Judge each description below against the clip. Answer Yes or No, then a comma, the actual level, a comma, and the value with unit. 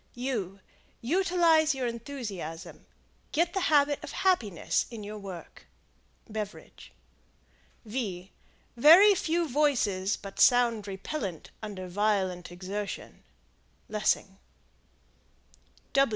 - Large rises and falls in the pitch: Yes, wide, 7.3 semitones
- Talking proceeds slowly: Yes, slow, 80 wpm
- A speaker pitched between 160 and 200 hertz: No, high, 220 Hz